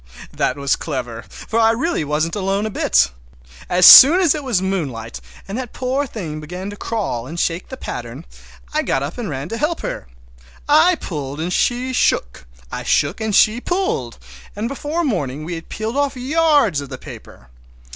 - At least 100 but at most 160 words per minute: No, average, 185 wpm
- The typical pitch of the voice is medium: No, high, 195 Hz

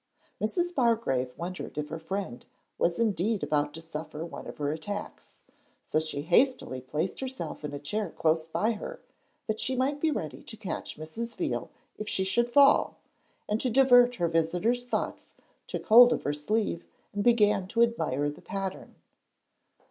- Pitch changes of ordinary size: No, wide, 6.8 semitones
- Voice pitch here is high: Yes, high, 200 Hz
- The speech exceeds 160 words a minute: Yes, average, 170 wpm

